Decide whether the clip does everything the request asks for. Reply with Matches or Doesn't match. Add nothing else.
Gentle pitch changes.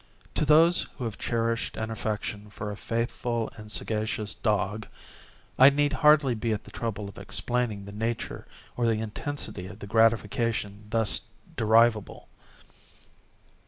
Matches